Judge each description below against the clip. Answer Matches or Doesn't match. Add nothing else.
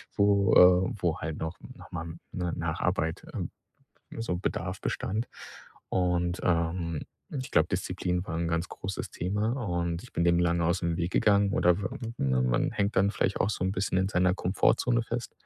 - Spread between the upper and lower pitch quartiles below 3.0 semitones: Matches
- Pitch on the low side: Matches